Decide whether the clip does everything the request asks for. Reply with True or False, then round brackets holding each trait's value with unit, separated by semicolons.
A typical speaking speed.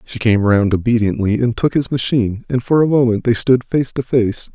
False (225 wpm)